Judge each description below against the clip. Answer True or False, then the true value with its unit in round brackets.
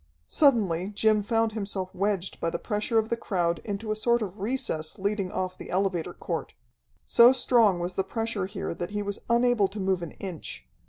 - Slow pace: False (195 wpm)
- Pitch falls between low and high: False (200 Hz)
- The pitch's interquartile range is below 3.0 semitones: False (3.3 semitones)